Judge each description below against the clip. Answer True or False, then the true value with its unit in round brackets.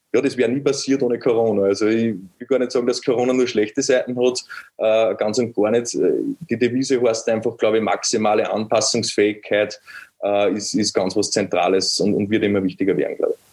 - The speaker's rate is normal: False (205 wpm)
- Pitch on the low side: True (115 Hz)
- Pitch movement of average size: True (3.4 semitones)